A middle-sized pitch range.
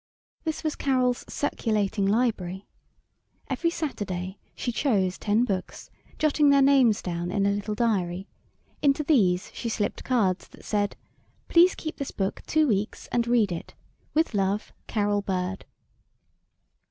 No: wide, 5.7 semitones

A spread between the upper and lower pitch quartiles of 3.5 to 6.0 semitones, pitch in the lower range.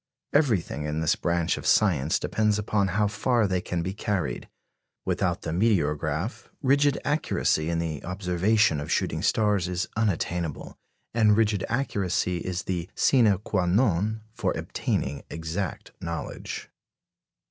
Yes: average, 4.4 semitones; very low, 95 Hz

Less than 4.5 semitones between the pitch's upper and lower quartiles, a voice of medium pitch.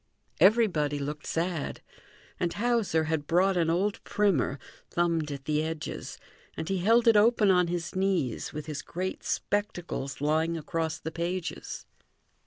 Yes: average, 3.8 semitones; medium, 170 Hz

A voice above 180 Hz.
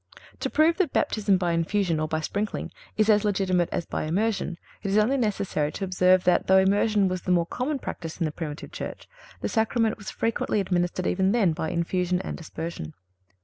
Yes: high, 190 Hz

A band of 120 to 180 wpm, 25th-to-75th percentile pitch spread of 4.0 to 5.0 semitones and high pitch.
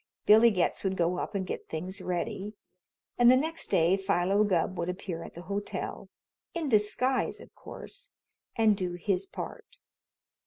No: average, 160 wpm; average, 3.2 semitones; high, 195 Hz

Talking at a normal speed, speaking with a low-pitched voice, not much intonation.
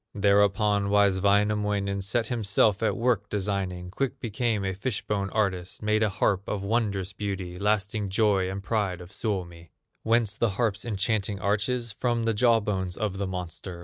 Yes: average, 165 wpm; low, 100 Hz; narrow, 2.1 semitones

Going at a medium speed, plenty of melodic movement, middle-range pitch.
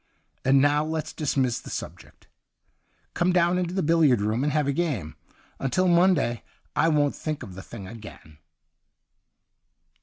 Yes: average, 150 wpm; wide, 6.0 semitones; medium, 145 Hz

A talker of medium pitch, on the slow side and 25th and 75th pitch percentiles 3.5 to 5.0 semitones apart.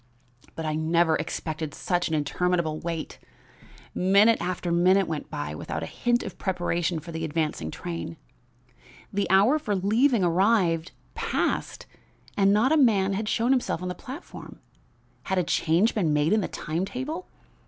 No: medium, 180 Hz; average, 160 wpm; average, 4.6 semitones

